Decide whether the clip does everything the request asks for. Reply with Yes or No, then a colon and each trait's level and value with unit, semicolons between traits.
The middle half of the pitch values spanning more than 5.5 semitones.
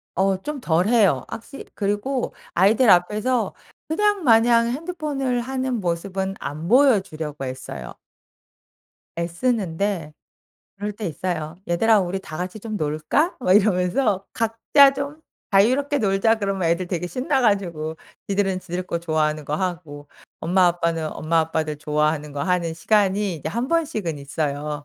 Yes: wide, 6.1 semitones